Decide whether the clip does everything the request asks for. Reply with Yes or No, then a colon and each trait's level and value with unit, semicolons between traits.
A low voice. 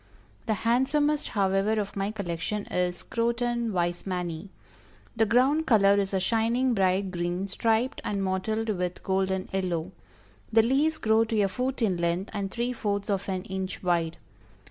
No: high, 200 Hz